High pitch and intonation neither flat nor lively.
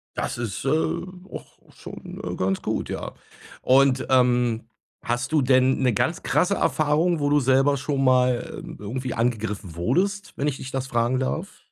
No: low, 130 Hz; average, 3.2 semitones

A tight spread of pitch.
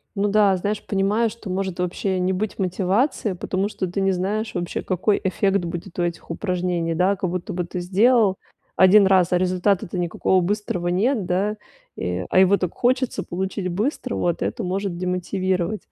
Yes: narrow, 2.3 semitones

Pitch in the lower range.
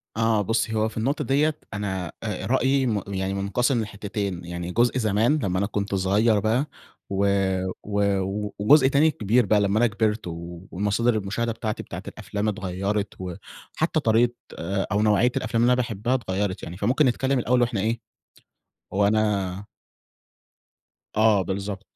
Yes: low, 105 Hz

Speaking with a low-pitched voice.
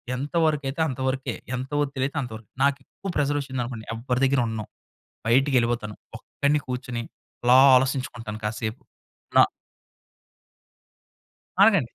Yes: low, 130 Hz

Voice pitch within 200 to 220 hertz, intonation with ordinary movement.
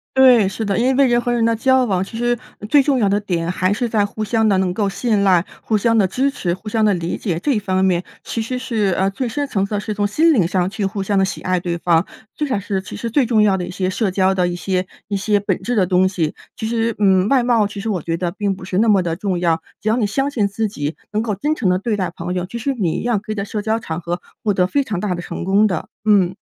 Yes: high, 205 Hz; average, 3.6 semitones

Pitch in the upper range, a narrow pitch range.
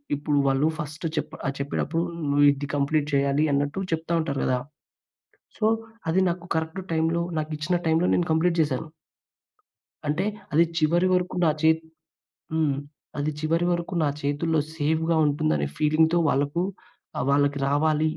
No: medium, 155 Hz; narrow, 2.3 semitones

